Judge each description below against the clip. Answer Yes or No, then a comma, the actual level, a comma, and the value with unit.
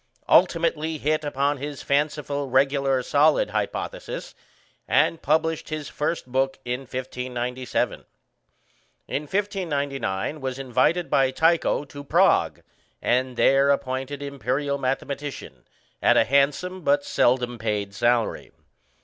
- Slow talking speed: Yes, slow, 110 wpm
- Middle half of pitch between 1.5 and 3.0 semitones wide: Yes, narrow, 2.6 semitones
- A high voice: No, medium, 140 Hz